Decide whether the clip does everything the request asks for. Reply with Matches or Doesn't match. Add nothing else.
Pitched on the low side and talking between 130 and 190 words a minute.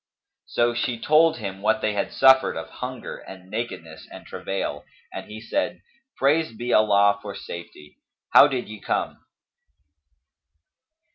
Matches